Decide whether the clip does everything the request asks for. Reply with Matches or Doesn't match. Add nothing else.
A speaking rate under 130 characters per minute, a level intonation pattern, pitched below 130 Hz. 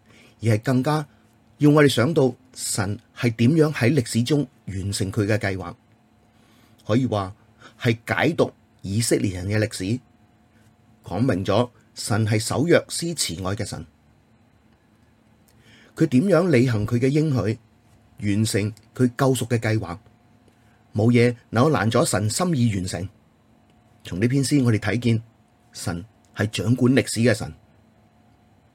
Doesn't match